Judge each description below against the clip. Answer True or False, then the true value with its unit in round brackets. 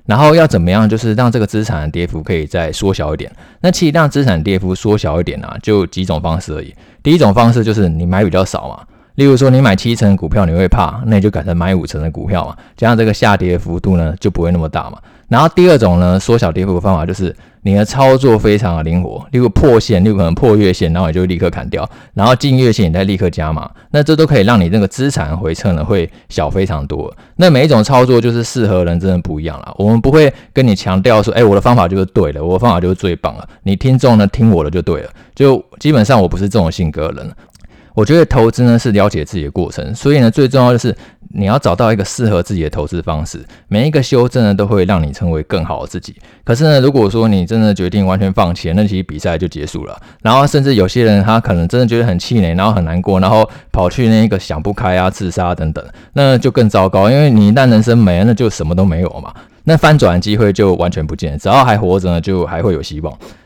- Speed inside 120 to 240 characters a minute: False (375 characters per minute)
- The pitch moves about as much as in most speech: True (4.9 semitones)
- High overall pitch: False (100 Hz)